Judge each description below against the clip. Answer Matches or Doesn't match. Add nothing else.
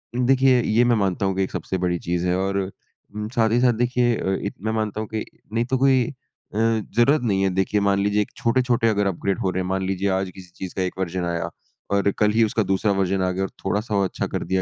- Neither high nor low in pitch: Doesn't match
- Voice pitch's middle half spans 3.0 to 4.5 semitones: Matches